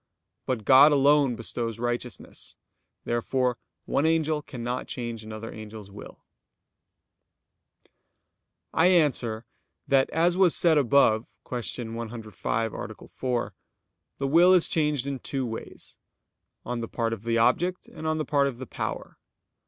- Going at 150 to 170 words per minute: No, slow, 135 wpm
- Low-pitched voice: Yes, low, 125 Hz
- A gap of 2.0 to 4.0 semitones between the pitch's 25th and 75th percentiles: No, average, 4.5 semitones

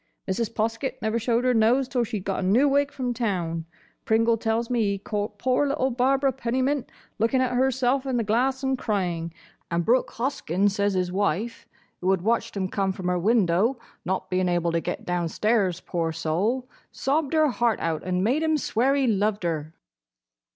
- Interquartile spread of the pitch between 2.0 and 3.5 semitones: No, wide, 5.4 semitones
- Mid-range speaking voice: No, high, 225 Hz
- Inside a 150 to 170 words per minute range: No, average, 190 wpm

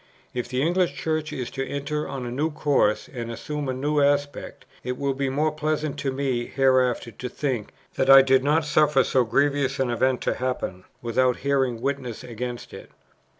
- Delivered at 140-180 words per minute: No, average, 190 wpm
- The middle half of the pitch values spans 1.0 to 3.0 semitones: Yes, narrow, 2.4 semitones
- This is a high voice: No, low, 135 Hz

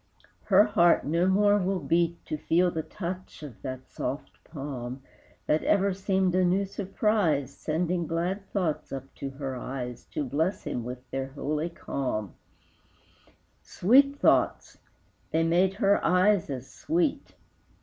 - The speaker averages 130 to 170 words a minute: Yes, average, 140 wpm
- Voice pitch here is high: No, medium, 170 Hz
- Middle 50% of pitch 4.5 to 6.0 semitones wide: Yes, wide, 5.6 semitones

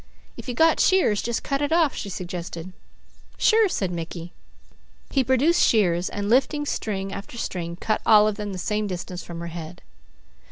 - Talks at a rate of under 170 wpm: No, average, 175 wpm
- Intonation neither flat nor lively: No, wide, 6.7 semitones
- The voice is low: No, high, 205 Hz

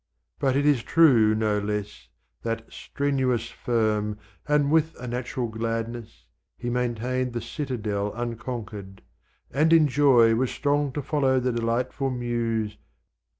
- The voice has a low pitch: Yes, low, 120 Hz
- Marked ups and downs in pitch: No, average, 3.2 semitones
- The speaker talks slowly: Yes, slow, 130 wpm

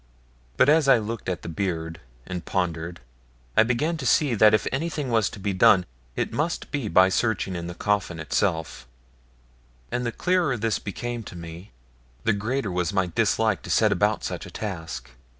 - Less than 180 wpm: No, average, 185 wpm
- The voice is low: Yes, low, 105 Hz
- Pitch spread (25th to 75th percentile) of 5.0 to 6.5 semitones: Yes, average, 5.3 semitones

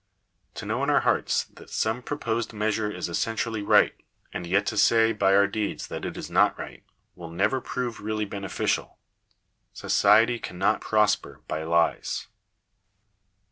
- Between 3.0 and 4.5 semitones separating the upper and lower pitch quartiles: No, narrow, 2.4 semitones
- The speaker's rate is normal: Yes, average, 150 wpm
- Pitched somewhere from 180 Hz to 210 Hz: No, low, 105 Hz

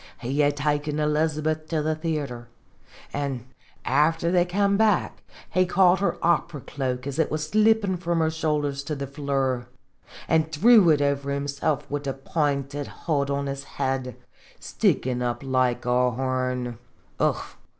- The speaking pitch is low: No, medium, 145 Hz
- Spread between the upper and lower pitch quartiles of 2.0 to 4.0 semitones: Yes, average, 3.1 semitones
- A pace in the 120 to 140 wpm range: No, average, 155 wpm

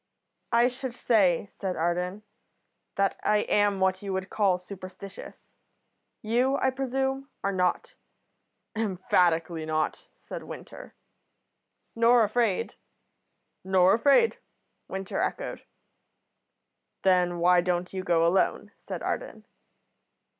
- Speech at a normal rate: No, slow, 105 wpm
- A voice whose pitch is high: Yes, high, 195 Hz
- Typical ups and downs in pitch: Yes, average, 4.3 semitones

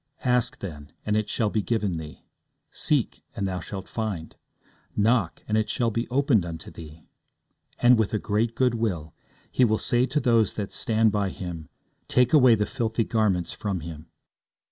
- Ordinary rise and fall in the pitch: Yes, average, 4.2 semitones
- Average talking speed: Yes, average, 170 wpm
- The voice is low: Yes, low, 110 Hz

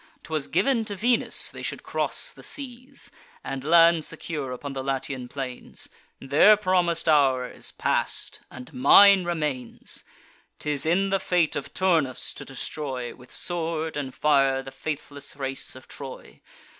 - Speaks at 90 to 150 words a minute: Yes, average, 145 wpm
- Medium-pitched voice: Yes, medium, 150 Hz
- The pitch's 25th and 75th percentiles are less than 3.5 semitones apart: No, average, 4.6 semitones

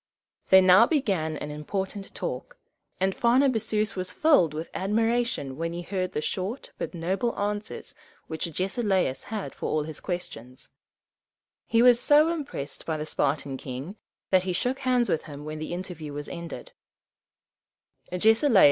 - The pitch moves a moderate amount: No, wide, 6.4 semitones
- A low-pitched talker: No, medium, 185 Hz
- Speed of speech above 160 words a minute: No, average, 145 wpm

